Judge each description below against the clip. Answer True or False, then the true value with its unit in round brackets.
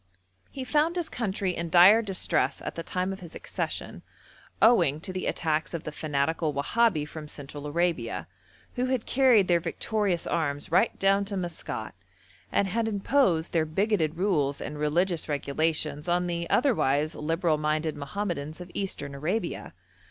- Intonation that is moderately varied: True (4.5 semitones)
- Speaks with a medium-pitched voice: True (170 Hz)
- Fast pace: False (155 wpm)